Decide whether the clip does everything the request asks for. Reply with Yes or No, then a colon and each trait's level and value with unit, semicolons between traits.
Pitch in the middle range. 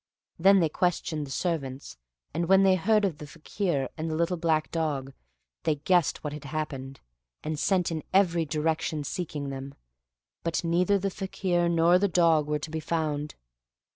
Yes: medium, 160 Hz